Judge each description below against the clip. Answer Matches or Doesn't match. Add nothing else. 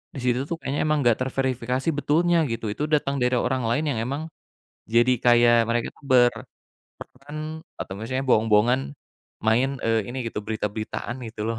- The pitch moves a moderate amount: Matches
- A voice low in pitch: Matches